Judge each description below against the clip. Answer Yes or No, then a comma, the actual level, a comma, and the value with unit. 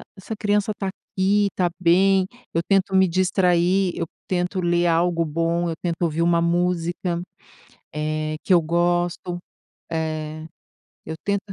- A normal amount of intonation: No, narrow, 2.1 semitones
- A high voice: No, medium, 175 Hz